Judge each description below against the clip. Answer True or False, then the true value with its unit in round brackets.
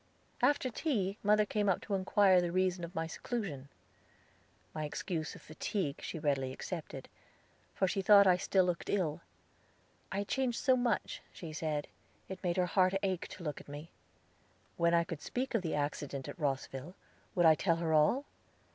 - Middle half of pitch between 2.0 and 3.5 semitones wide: False (4.3 semitones)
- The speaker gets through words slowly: False (180 wpm)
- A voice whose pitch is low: False (180 Hz)